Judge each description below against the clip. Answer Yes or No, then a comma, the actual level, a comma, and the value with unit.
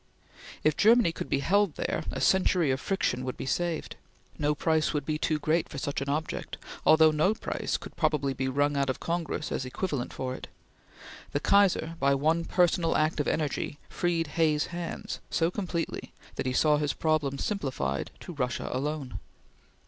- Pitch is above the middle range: No, medium, 155 Hz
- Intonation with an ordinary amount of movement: Yes, average, 3.3 semitones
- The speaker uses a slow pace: No, average, 180 wpm